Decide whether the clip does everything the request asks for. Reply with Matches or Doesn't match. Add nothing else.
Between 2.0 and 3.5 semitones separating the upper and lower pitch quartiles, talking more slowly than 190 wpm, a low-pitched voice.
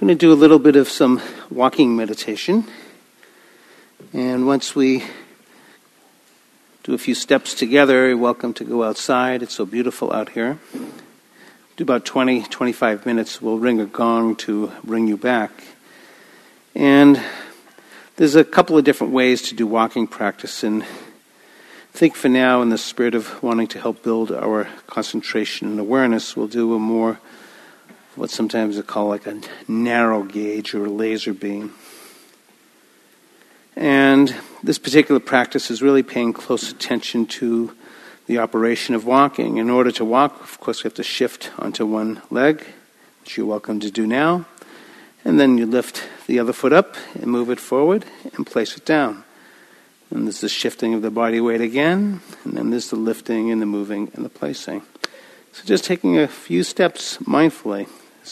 Matches